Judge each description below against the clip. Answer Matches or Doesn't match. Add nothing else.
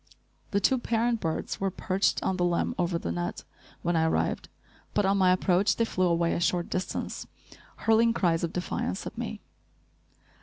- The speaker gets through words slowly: Doesn't match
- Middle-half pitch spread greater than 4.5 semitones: Doesn't match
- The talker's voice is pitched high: Doesn't match